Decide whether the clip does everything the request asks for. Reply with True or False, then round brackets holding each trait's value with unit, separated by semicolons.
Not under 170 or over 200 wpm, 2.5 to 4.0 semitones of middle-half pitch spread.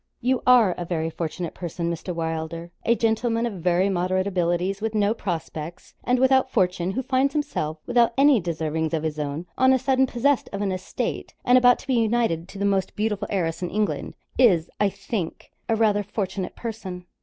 False (190 wpm; 5.4 semitones)